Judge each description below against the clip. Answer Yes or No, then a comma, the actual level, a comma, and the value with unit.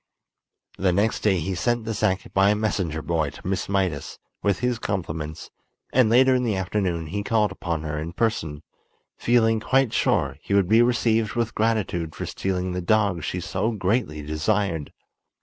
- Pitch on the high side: No, very low, 95 Hz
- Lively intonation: No, average, 4.7 semitones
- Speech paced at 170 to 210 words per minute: Yes, average, 175 wpm